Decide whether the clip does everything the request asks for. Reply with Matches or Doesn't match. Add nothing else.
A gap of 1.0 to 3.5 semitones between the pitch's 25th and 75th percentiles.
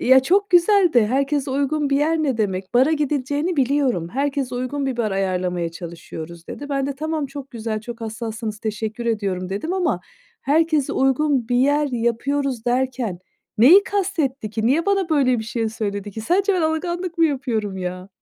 Doesn't match